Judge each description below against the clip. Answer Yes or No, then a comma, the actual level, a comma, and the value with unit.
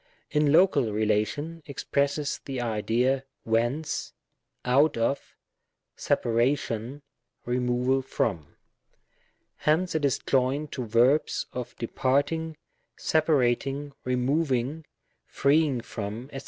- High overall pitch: No, low, 135 Hz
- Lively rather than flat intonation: No, average, 3.5 semitones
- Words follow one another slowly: Yes, slow, 90 wpm